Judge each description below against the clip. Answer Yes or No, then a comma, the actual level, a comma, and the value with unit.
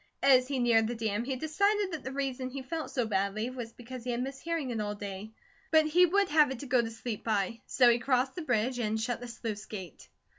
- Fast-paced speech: Yes, fast, 250 wpm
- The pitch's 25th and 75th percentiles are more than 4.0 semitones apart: No, average, 3.7 semitones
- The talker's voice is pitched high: Yes, very high, 250 Hz